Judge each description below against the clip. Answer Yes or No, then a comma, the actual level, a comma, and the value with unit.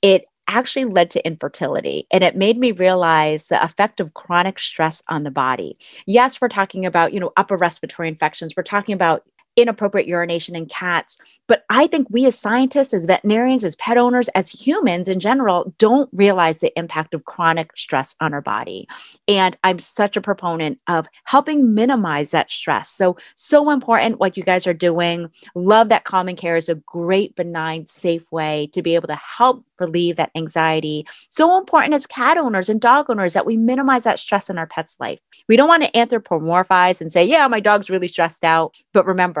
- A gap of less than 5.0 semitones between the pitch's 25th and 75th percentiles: No, wide, 5.5 semitones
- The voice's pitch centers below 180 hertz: No, medium, 185 Hz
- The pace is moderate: Yes, average, 195 wpm